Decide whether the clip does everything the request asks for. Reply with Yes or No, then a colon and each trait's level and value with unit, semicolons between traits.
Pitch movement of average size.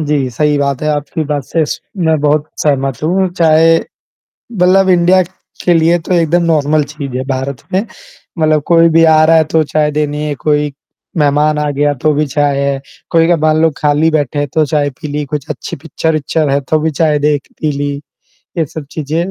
No: narrow, 1.9 semitones